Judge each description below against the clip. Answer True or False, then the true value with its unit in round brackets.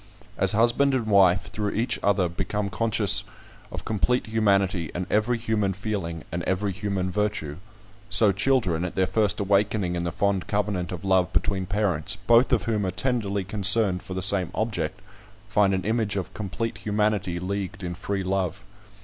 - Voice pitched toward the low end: True (100 Hz)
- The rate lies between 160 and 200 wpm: True (170 wpm)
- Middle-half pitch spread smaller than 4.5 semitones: True (2.5 semitones)